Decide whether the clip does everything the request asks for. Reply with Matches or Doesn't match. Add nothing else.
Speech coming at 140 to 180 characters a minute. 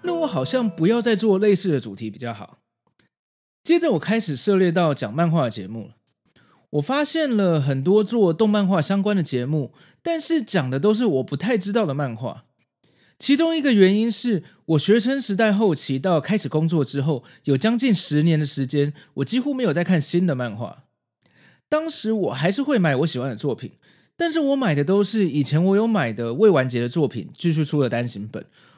Doesn't match